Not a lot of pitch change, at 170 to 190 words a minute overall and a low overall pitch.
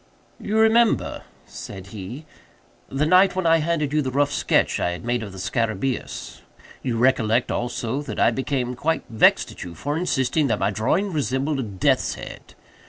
No: average, 5.3 semitones; average, 175 wpm; low, 130 Hz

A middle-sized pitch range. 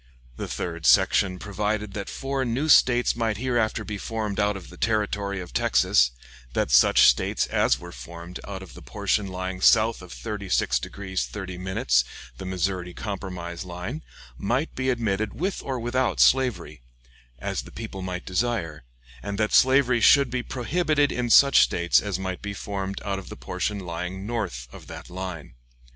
Yes: average, 4.4 semitones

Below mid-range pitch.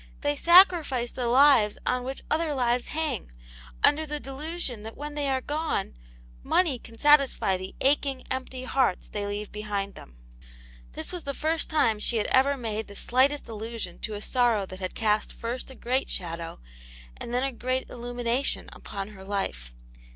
No: very high, 250 Hz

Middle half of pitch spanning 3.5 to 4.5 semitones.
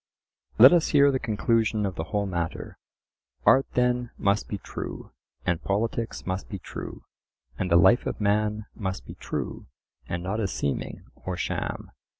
Yes: average, 3.8 semitones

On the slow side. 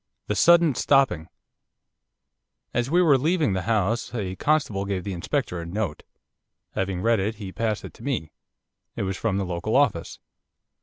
No: average, 165 wpm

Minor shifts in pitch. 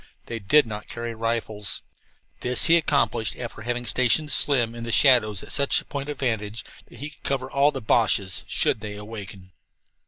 No: average, 4.3 semitones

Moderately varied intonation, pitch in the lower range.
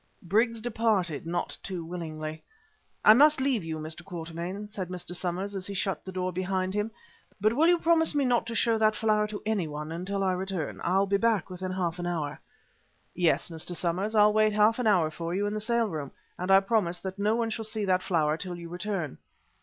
No: average, 3.8 semitones; high, 190 Hz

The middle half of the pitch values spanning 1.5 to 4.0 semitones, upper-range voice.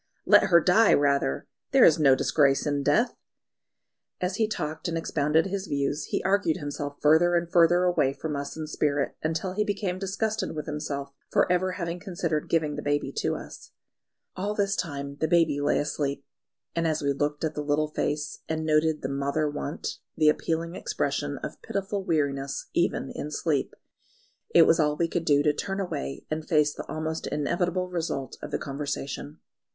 No: average, 3.2 semitones; medium, 155 Hz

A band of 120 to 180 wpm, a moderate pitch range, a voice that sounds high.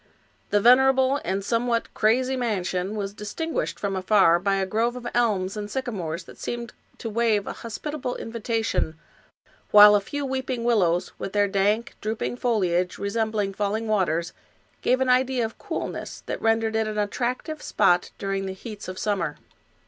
Yes: average, 165 wpm; average, 3.4 semitones; high, 215 Hz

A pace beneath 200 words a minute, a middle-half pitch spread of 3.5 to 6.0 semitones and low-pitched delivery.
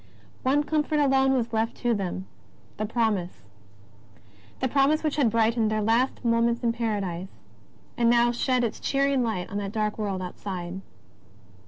No: average, 160 wpm; average, 3.9 semitones; high, 230 Hz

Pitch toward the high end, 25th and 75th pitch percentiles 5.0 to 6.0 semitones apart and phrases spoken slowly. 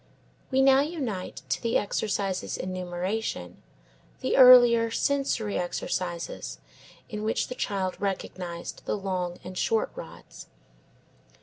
Yes: high, 205 Hz; wide, 5.5 semitones; slow, 115 wpm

